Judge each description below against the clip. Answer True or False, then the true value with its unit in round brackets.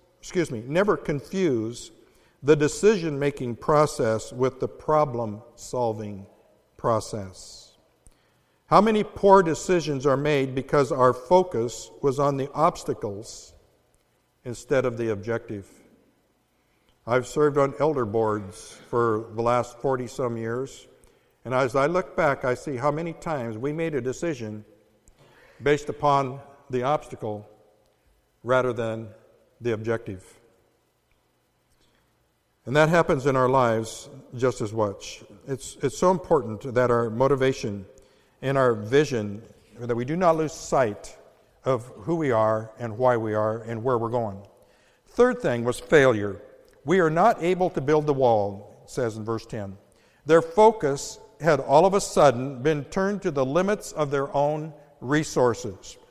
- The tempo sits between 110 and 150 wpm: True (140 wpm)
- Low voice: True (130 Hz)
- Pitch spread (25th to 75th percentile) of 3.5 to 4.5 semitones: False (4.9 semitones)